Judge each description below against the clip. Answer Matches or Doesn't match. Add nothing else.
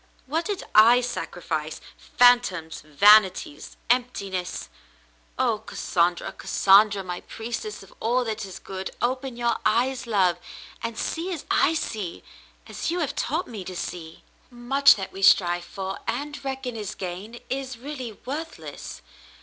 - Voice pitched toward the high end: Matches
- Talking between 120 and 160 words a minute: Matches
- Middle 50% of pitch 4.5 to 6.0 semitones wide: Matches